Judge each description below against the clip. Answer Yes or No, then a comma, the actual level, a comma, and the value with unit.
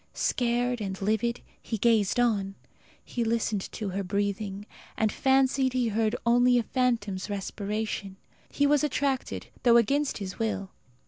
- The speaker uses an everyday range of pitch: Yes, average, 3.5 semitones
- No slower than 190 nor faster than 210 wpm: No, average, 140 wpm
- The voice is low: No, high, 225 Hz